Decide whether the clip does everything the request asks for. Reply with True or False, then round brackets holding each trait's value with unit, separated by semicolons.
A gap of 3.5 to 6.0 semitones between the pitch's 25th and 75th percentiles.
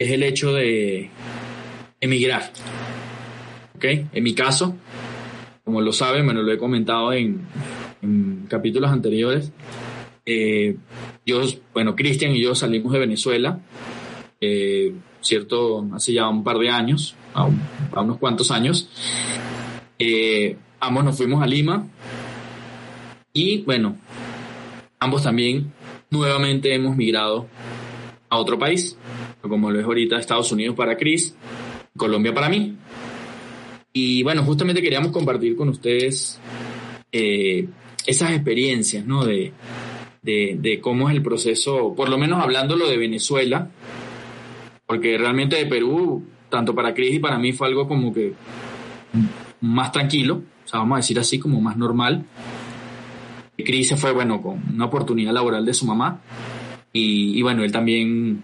False (3.1 semitones)